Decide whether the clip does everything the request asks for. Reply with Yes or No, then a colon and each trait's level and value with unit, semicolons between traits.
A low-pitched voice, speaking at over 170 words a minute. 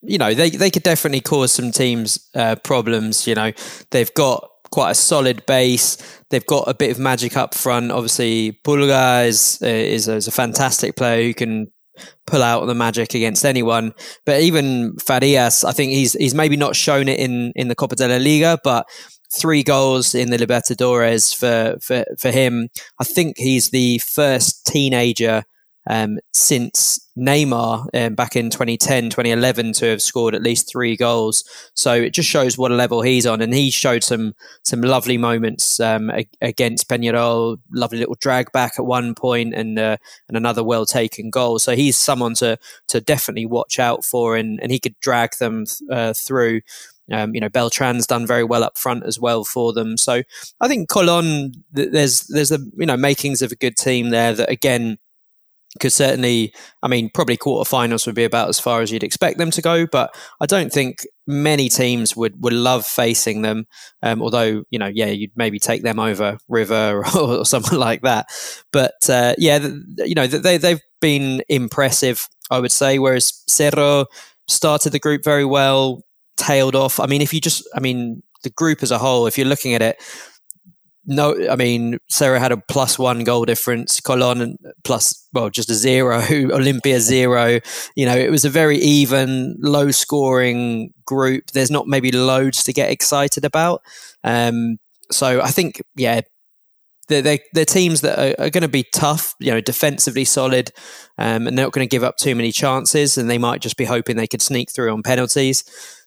Yes: low, 125 Hz; average, 190 wpm